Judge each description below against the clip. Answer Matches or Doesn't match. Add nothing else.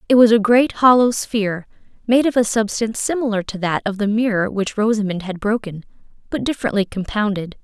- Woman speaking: Matches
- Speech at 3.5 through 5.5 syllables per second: Doesn't match